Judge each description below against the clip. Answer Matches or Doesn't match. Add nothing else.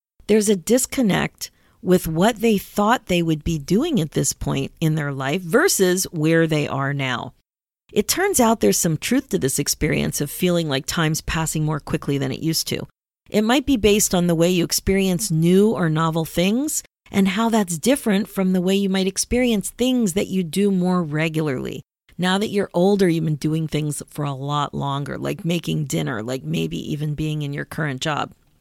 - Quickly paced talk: Doesn't match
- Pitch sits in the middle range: Matches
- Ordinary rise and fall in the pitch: Matches